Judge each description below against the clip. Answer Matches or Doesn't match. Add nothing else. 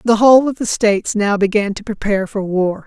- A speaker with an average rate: Doesn't match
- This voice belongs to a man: Doesn't match